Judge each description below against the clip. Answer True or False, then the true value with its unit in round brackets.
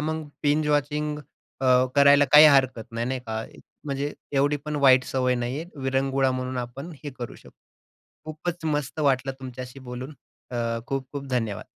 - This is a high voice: False (135 Hz)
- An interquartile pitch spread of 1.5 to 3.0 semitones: True (2.5 semitones)